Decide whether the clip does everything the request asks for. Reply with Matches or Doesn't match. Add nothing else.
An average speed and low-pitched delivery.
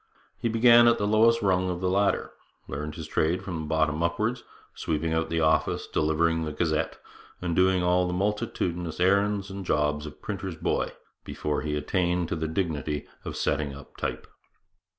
Matches